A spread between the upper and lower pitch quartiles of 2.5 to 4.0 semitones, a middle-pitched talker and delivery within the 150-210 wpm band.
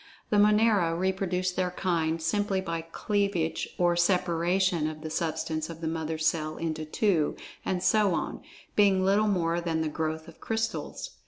Yes: average, 3.1 semitones; medium, 175 Hz; average, 160 wpm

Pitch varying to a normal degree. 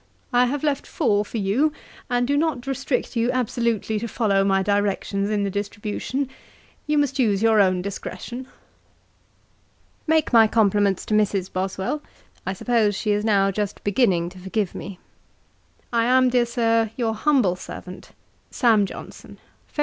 Yes: average, 3.8 semitones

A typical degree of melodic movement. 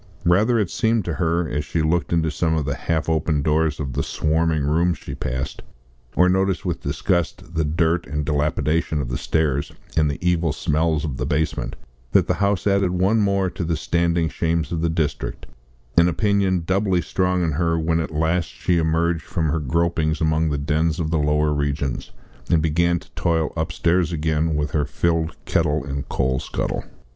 No: narrow, 2.2 semitones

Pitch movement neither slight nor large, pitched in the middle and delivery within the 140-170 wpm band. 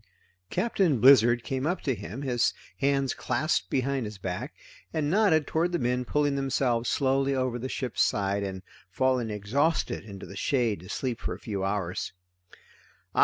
No: average, 4.7 semitones; low, 130 Hz; average, 165 wpm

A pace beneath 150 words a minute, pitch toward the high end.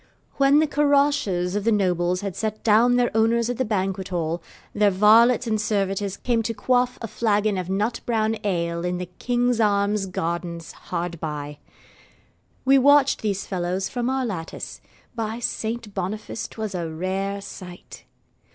No: average, 155 wpm; high, 205 Hz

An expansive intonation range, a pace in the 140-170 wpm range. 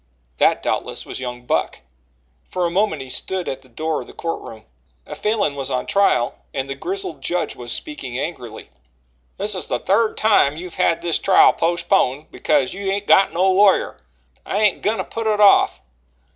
No: wide, 6.6 semitones; average, 190 wpm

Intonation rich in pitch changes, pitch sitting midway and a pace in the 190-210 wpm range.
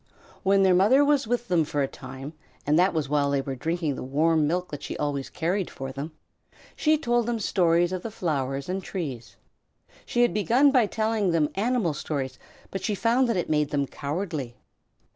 Yes: wide, 6.9 semitones; medium, 170 Hz; average, 200 wpm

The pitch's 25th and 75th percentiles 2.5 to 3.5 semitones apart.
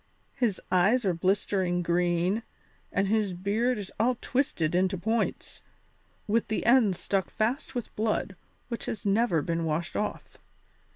No: average, 4.2 semitones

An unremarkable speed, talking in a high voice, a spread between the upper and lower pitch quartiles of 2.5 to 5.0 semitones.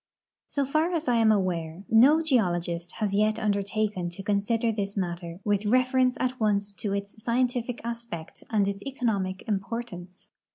Yes: average, 160 wpm; high, 210 Hz; average, 3.6 semitones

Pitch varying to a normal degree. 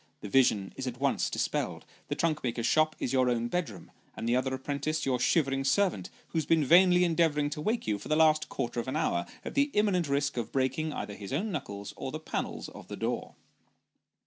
Yes: average, 4.6 semitones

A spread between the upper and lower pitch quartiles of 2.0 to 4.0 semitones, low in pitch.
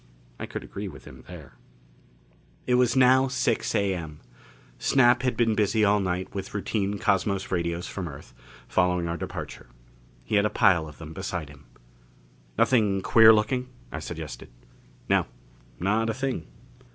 No: average, 4.4 semitones; low, 100 Hz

